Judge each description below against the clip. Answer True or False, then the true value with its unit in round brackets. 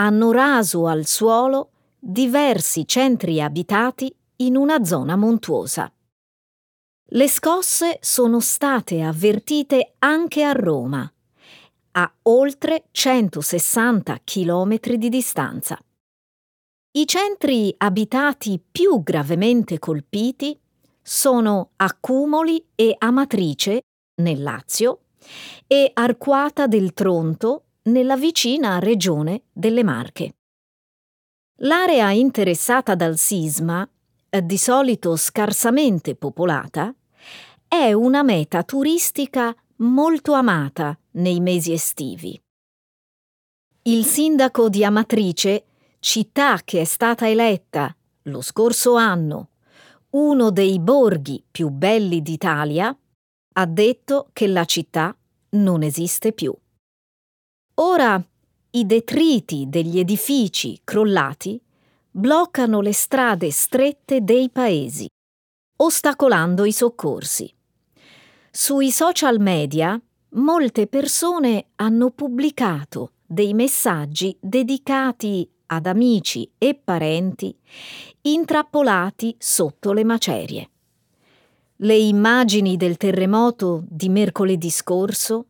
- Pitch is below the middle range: False (220 Hz)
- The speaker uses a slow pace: True (90 wpm)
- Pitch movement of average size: False (6.6 semitones)